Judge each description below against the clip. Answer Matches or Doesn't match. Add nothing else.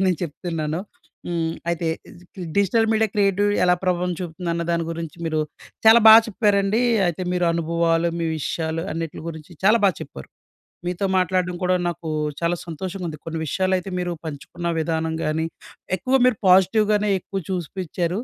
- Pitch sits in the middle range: Matches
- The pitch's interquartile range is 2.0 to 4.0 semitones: Matches